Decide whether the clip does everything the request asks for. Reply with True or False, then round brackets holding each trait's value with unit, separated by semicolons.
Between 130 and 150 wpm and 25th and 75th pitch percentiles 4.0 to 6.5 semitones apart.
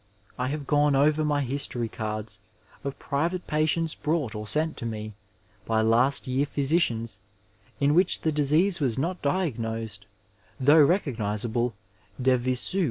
True (140 wpm; 5.1 semitones)